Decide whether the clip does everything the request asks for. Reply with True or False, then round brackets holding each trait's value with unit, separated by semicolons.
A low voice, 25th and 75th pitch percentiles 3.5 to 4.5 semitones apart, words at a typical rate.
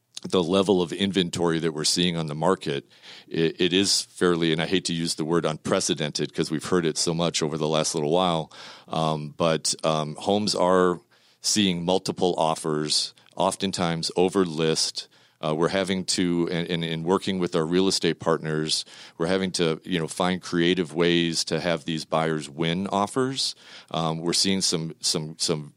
False (85 Hz; 2.5 semitones; 180 wpm)